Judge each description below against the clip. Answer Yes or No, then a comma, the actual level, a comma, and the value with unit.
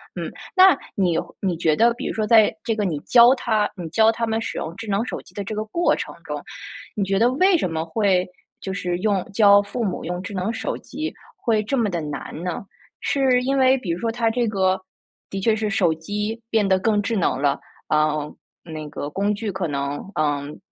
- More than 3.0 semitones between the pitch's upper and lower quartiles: Yes, average, 4.3 semitones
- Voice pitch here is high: Yes, high, 205 Hz